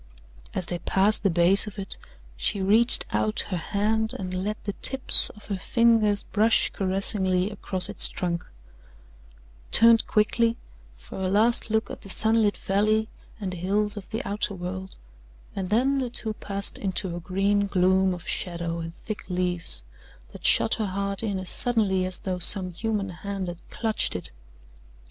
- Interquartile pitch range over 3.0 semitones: No, average, 2.7 semitones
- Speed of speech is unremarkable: Yes, average, 165 wpm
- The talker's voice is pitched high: Yes, high, 200 Hz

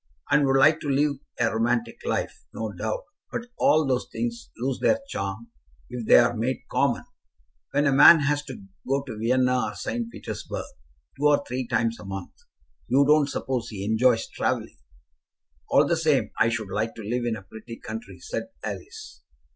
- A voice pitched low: Yes, low, 125 Hz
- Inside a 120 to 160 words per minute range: No, average, 180 wpm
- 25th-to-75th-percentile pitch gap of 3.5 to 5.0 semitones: Yes, average, 4.0 semitones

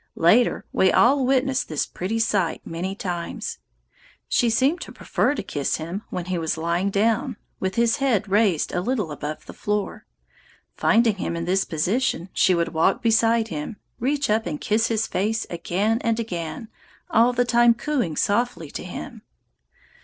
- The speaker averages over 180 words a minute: No, average, 170 wpm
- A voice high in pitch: Yes, high, 210 Hz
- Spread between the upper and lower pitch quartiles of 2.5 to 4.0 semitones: No, average, 5.3 semitones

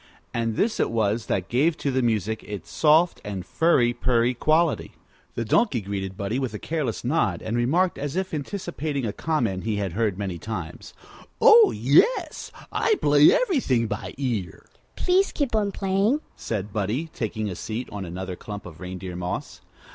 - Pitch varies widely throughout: Yes, wide, 7.8 semitones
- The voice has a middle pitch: No, low, 120 Hz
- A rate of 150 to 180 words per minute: Yes, average, 170 wpm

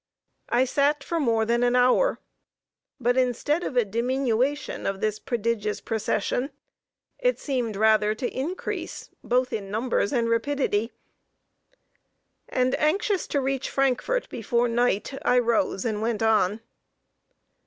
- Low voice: No, high, 245 Hz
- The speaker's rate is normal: No, slow, 130 wpm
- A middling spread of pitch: Yes, average, 3.5 semitones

